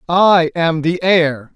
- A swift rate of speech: No, average, 155 wpm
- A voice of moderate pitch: Yes, medium, 165 Hz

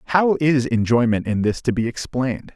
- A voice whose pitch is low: Yes, low, 125 Hz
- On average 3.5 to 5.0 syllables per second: No, 5.4 syllables/s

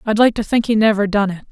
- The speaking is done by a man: No, female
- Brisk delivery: Yes, fast, 315 wpm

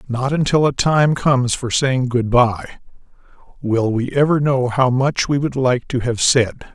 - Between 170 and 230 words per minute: Yes, average, 185 wpm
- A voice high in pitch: No, low, 130 Hz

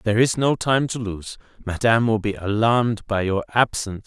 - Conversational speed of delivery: Yes, average, 190 wpm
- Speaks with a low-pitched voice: Yes, low, 110 Hz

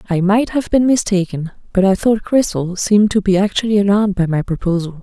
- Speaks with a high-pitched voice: Yes, high, 200 Hz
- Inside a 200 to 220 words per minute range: Yes, fast, 205 wpm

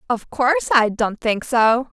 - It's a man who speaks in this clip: No, female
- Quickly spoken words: No, average, 180 wpm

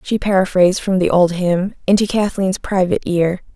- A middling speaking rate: Yes, average, 170 wpm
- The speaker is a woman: Yes, female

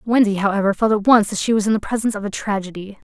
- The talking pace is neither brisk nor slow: No, fast, 270 wpm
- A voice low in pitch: No, high, 210 Hz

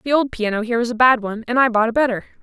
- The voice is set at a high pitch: Yes, high, 235 Hz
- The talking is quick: Yes, fast, 320 wpm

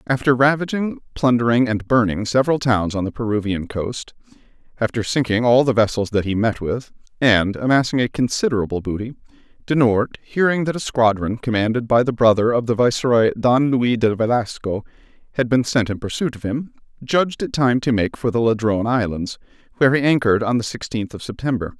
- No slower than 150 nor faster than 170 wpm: No, average, 180 wpm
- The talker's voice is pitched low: Yes, low, 120 Hz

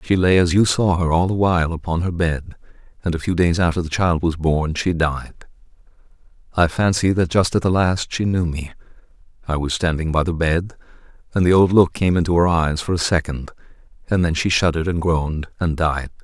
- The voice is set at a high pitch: No, very low, 85 Hz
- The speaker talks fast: Yes, fast, 215 wpm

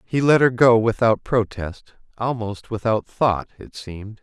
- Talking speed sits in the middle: Yes, average, 155 wpm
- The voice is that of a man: Yes, male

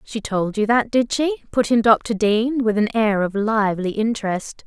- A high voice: Yes, high, 220 Hz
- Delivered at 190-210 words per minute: Yes, fast, 205 wpm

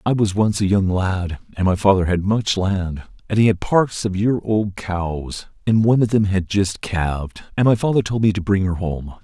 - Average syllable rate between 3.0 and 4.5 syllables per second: No, 4.8 syllables/s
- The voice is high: No, low, 100 Hz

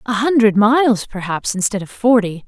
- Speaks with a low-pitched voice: No, high, 220 Hz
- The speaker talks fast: No, average, 170 wpm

